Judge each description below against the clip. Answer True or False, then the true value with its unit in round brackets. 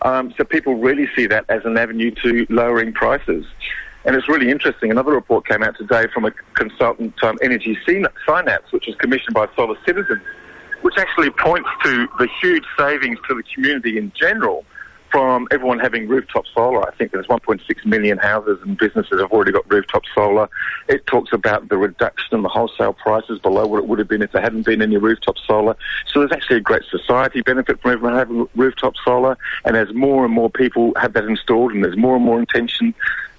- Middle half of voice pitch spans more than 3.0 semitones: False (2.7 semitones)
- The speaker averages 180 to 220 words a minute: True (200 wpm)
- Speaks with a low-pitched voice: True (125 Hz)